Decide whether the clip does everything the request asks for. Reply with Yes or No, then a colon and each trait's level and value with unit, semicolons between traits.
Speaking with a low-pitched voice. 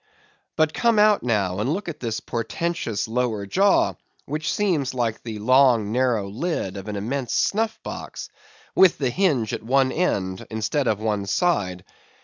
Yes: low, 125 Hz